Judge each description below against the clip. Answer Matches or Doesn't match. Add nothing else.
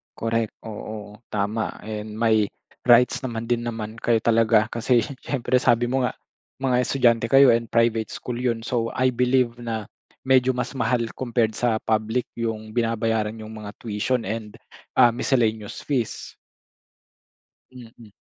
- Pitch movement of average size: Doesn't match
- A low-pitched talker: Matches